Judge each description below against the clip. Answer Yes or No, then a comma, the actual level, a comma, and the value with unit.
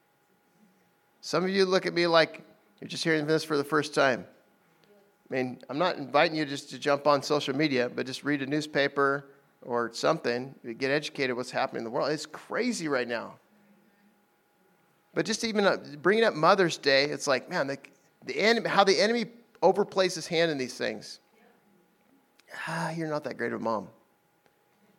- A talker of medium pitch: Yes, medium, 155 Hz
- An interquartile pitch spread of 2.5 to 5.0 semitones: No, wide, 5.5 semitones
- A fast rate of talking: No, average, 180 wpm